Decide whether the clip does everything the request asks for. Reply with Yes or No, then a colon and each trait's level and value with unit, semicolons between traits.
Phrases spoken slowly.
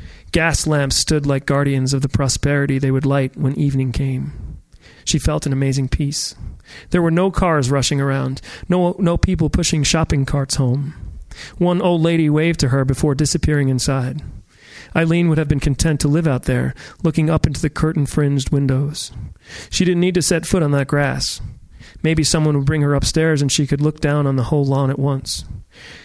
No: average, 190 wpm